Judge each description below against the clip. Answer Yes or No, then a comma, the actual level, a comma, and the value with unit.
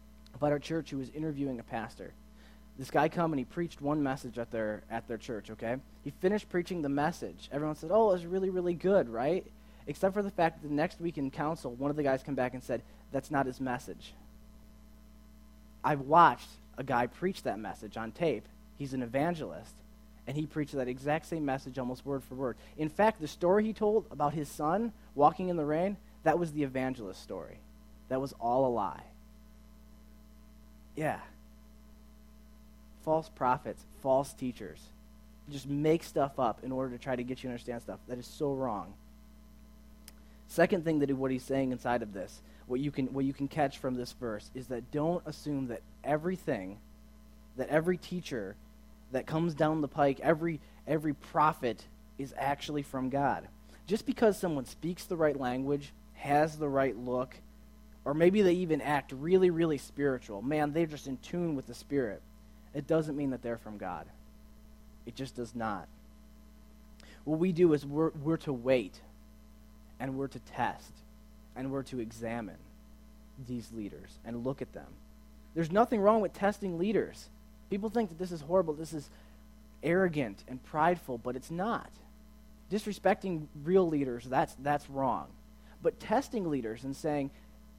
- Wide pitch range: Yes, wide, 6.9 semitones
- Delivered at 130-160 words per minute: No, average, 175 wpm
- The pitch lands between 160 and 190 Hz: No, low, 135 Hz